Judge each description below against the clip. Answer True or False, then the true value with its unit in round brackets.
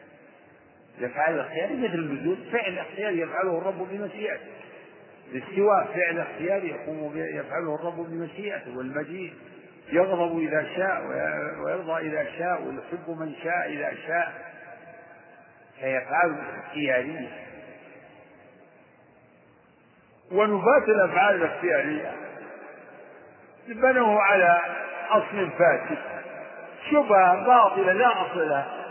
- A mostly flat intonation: False (3.3 semitones)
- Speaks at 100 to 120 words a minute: False (85 wpm)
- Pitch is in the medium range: True (175 Hz)